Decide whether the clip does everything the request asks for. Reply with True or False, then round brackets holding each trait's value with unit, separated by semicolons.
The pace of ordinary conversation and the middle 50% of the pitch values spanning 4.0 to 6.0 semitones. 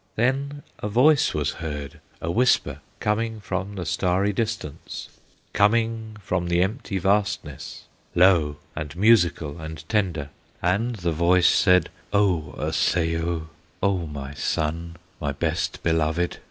False (125 wpm; 4.7 semitones)